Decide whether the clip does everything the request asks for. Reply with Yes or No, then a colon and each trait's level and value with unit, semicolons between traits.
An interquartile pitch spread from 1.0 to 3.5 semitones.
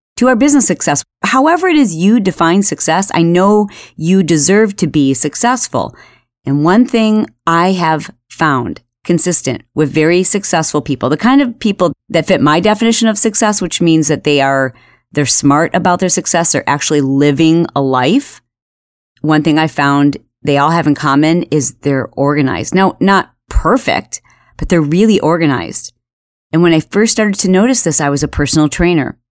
No: average, 5.2 semitones